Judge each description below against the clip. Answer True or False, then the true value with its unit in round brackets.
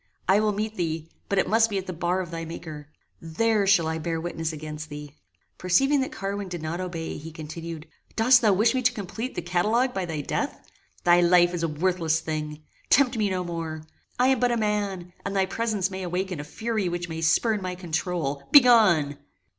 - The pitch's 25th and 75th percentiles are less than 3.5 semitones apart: False (4.5 semitones)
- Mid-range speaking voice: True (180 Hz)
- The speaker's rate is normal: False (210 wpm)